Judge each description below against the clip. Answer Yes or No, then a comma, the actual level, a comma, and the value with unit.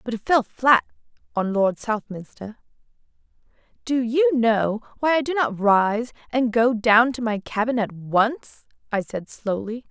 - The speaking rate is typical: Yes, average, 160 wpm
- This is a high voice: Yes, high, 230 Hz